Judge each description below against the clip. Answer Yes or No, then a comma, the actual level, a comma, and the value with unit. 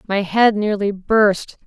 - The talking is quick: No, average, 145 wpm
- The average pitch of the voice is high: Yes, high, 205 Hz